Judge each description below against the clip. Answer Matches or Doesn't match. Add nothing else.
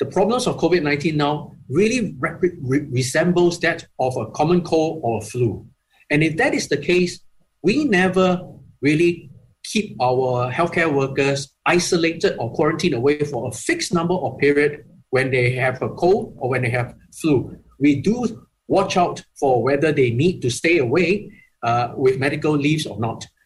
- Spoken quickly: Doesn't match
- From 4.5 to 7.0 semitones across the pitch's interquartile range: Matches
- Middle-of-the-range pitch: Matches